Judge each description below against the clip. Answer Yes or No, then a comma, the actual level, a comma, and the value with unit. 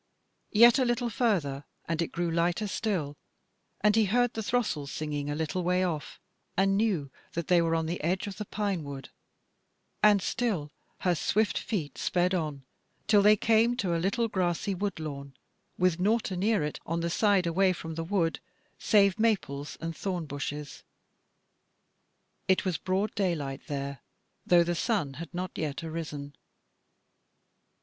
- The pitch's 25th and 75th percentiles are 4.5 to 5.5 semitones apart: Yes, average, 4.8 semitones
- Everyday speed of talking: Yes, average, 160 wpm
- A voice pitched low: No, medium, 175 Hz